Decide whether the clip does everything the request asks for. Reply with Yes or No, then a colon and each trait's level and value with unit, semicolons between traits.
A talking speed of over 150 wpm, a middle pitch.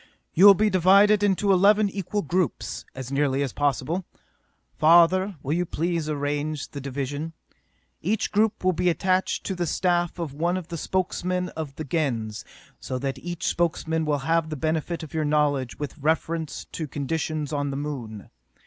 Yes: average, 170 wpm; medium, 160 Hz